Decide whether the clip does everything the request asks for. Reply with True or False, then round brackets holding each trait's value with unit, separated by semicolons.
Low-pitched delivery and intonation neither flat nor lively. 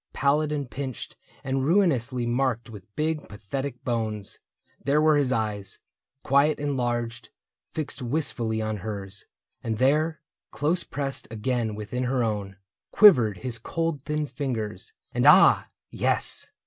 True (125 Hz; 4.7 semitones)